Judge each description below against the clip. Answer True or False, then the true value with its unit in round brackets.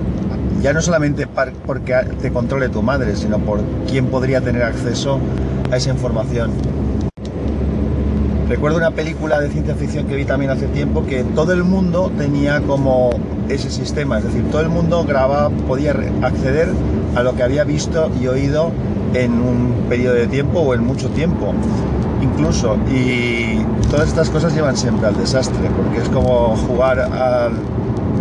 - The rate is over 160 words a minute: False (155 wpm)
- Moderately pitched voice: False (115 Hz)